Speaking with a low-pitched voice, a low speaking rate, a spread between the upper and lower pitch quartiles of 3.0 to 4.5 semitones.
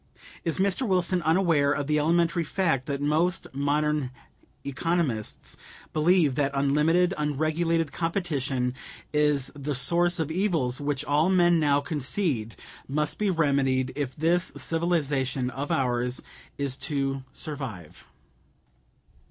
No: medium, 150 Hz; slow, 120 wpm; average, 3.6 semitones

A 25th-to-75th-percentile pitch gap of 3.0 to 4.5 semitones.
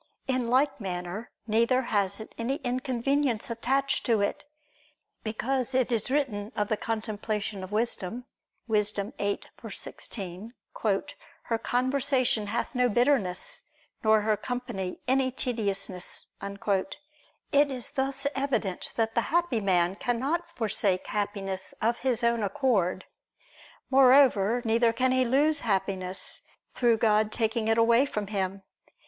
Yes: average, 4.0 semitones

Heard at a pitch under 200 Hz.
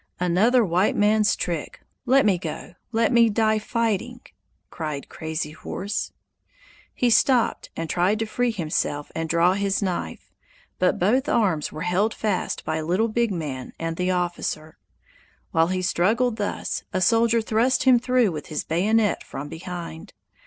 Yes: high, 190 Hz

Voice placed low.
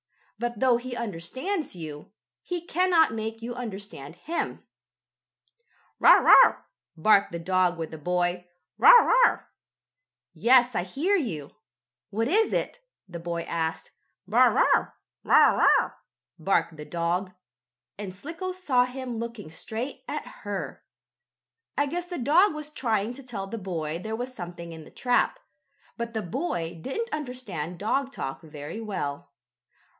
No: high, 220 Hz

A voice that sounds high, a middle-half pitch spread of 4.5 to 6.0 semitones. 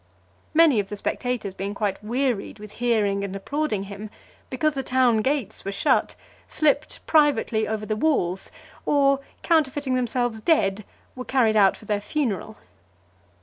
Yes: high, 225 Hz; average, 4.9 semitones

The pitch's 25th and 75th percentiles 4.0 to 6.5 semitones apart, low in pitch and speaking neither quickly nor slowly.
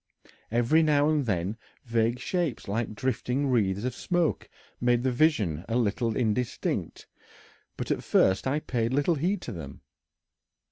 Yes: average, 4.7 semitones; low, 120 Hz; average, 145 wpm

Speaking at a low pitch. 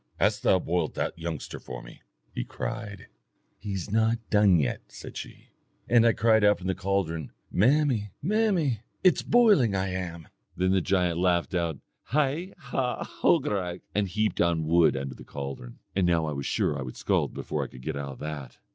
Yes: very low, 95 Hz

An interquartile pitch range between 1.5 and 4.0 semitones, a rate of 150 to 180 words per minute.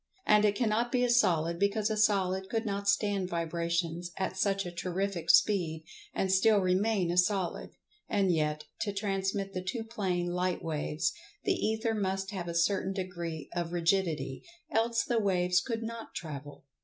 Yes: average, 3.3 semitones; average, 165 wpm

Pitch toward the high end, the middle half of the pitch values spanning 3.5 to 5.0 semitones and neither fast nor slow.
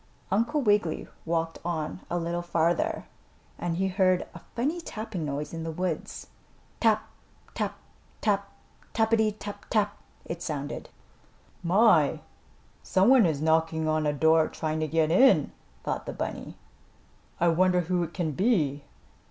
No: medium, 175 Hz; average, 4.3 semitones; average, 145 wpm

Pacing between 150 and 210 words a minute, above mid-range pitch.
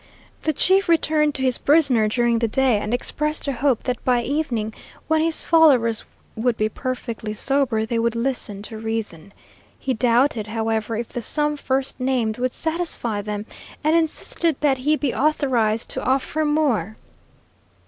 Yes: average, 160 wpm; very high, 255 Hz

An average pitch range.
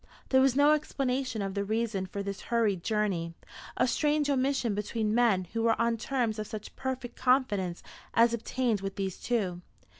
Yes: average, 4.3 semitones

